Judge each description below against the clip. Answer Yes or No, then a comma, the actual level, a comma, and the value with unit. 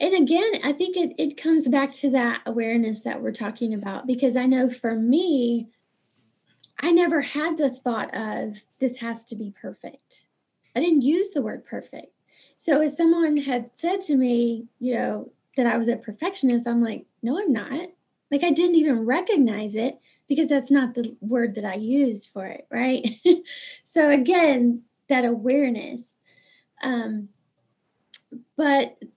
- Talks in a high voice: Yes, very high, 260 Hz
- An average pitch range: Yes, average, 4.4 semitones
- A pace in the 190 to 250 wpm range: No, average, 165 wpm